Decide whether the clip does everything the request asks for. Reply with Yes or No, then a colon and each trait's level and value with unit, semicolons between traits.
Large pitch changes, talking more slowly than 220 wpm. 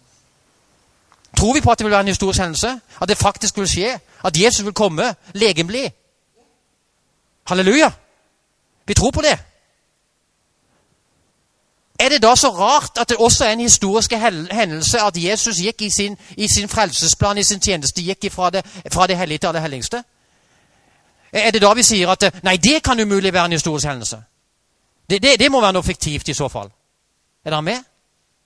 No: average, 4.2 semitones; average, 175 wpm